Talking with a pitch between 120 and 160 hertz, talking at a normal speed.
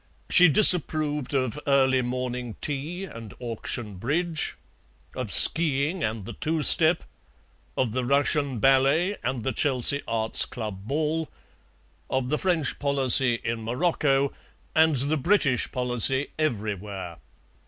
No: low, 135 Hz; slow, 125 wpm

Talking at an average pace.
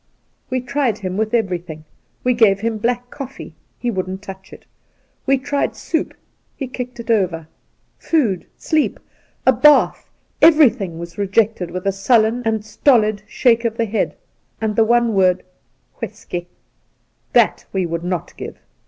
Yes: average, 165 wpm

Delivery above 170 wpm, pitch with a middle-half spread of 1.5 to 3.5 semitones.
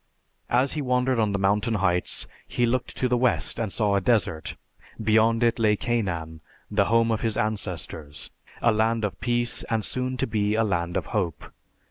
Yes: average, 185 wpm; average, 3.0 semitones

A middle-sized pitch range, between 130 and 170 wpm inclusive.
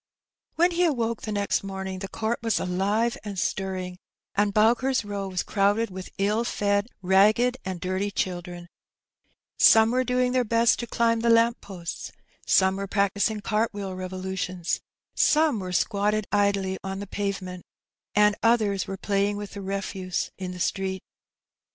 Yes: average, 3.0 semitones; average, 160 wpm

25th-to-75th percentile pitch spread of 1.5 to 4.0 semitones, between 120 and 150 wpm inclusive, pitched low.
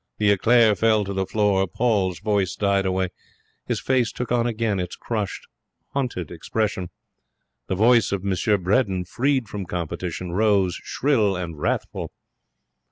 Yes: average, 3.4 semitones; average, 145 wpm; low, 100 Hz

